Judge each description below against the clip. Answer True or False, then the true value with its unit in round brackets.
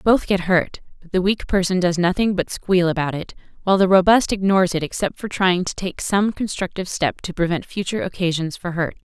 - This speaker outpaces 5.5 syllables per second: True (5.7 syllables/s)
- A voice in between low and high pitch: True (180 Hz)